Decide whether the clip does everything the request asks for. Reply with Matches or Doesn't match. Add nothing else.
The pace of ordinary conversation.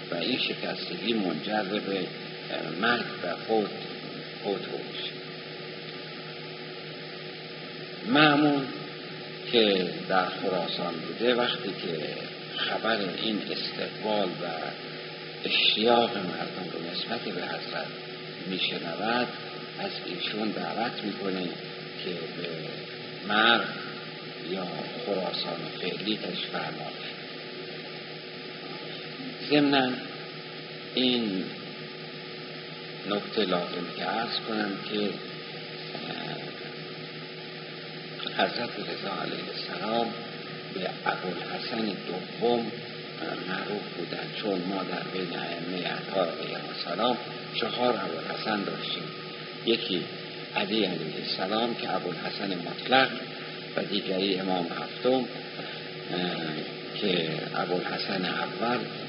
Doesn't match